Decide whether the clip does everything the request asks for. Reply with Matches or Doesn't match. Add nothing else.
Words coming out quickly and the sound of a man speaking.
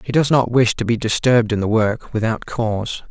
Matches